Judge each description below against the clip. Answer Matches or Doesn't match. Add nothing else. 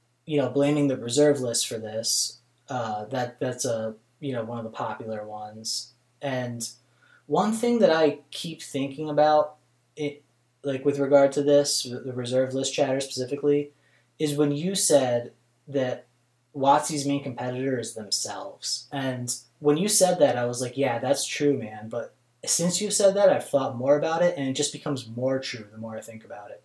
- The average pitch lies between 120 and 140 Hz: Matches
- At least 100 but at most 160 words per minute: Doesn't match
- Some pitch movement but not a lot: Matches